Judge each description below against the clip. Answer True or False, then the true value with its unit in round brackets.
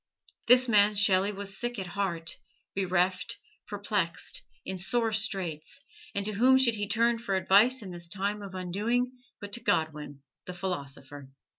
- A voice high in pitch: True (200 Hz)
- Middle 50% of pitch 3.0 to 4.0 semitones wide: True (3.5 semitones)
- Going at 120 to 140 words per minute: False (155 wpm)